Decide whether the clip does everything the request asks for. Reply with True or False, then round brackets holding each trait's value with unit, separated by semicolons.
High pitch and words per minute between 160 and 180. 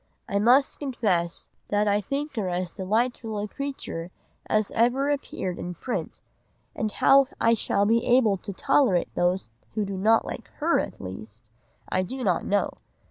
True (210 Hz; 165 wpm)